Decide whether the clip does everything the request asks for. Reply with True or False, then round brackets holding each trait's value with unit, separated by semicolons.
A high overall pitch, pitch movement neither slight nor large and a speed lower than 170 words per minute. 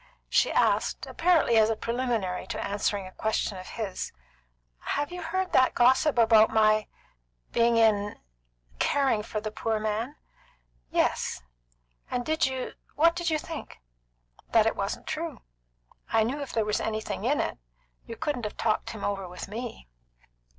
True (225 Hz; 4.4 semitones; 155 wpm)